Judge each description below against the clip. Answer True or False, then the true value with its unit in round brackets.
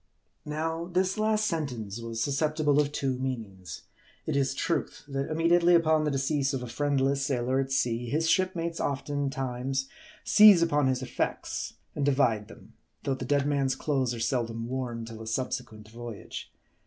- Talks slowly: False (160 wpm)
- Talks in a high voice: False (135 Hz)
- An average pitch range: True (3.8 semitones)